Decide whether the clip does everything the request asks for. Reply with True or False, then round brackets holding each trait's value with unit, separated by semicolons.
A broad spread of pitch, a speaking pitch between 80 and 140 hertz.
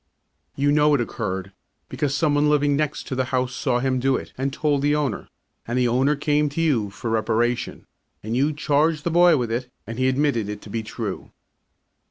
False (3.8 semitones; 135 Hz)